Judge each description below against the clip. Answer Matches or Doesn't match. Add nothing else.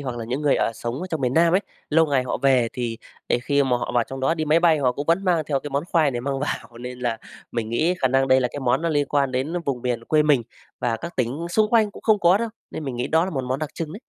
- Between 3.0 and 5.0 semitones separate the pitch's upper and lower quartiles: Matches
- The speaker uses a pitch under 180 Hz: Matches